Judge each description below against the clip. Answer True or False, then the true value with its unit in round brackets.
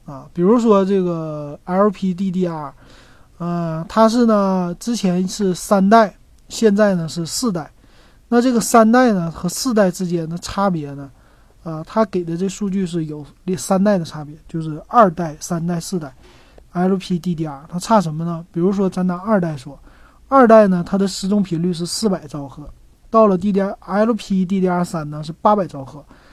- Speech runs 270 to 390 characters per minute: False (255 characters per minute)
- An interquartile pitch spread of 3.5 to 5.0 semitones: True (3.8 semitones)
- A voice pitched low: False (185 Hz)